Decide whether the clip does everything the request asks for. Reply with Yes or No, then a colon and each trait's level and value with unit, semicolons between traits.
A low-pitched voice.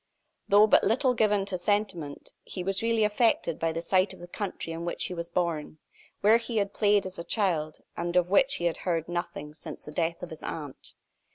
No: medium, 180 Hz